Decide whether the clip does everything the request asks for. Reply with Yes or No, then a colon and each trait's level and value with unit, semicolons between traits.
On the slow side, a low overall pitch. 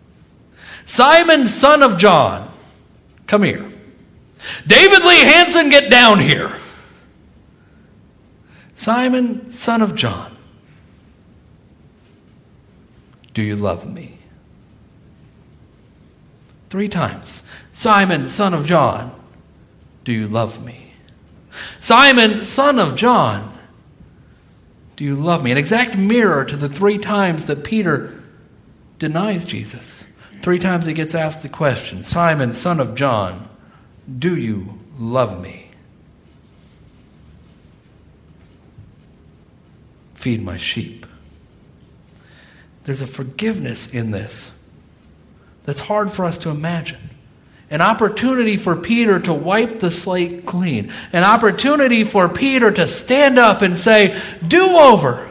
No: slow, 105 wpm; medium, 175 Hz